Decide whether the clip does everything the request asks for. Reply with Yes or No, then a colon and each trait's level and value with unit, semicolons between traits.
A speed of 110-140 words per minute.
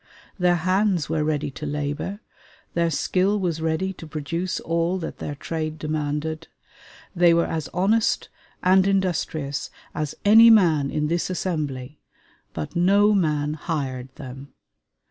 Yes: slow, 135 wpm